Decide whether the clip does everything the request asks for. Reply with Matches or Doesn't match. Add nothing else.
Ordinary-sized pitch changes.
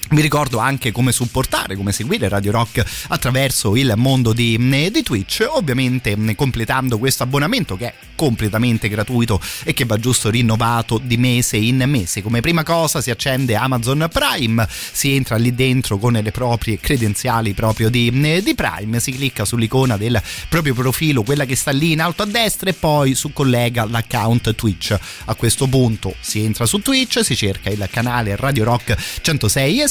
Matches